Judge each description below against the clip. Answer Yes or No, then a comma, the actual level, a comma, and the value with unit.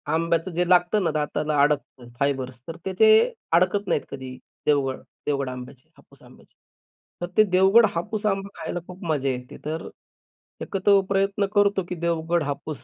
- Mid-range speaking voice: Yes, medium, 165 Hz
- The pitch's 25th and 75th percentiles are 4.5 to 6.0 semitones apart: Yes, average, 5.3 semitones